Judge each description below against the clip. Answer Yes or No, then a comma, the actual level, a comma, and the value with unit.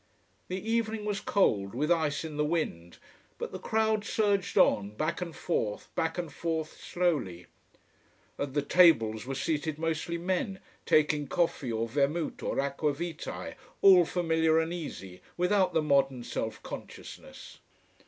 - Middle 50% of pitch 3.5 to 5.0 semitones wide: Yes, average, 4.3 semitones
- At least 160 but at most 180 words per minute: No, average, 145 wpm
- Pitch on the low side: No, medium, 160 Hz